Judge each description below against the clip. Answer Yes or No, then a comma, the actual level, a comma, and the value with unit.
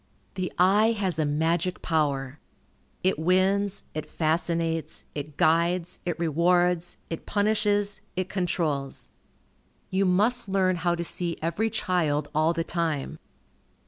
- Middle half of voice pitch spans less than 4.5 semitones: Yes, average, 2.8 semitones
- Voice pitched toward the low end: No, medium, 175 Hz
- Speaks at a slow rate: Yes, slow, 125 wpm